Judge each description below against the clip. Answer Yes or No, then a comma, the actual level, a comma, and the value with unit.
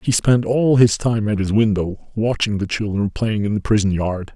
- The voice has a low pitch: Yes, low, 105 Hz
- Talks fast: Yes, fast, 220 wpm